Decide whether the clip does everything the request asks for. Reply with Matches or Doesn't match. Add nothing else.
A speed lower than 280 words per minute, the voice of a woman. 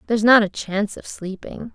Matches